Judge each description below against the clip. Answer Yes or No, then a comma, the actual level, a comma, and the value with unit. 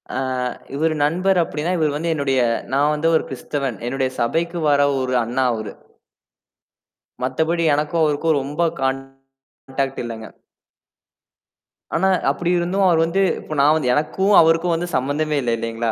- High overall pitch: No, medium, 150 Hz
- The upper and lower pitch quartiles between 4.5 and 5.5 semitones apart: No, average, 3.8 semitones